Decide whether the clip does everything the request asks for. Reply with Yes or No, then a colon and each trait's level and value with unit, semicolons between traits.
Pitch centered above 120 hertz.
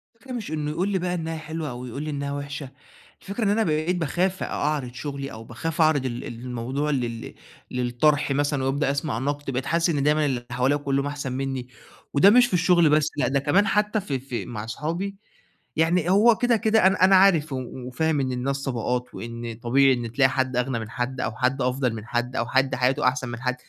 Yes: medium, 140 Hz